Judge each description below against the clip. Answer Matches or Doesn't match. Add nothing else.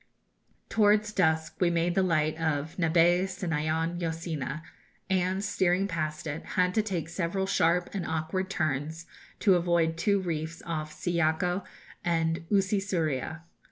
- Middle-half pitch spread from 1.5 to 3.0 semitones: Matches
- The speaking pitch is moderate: Matches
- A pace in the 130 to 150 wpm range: Matches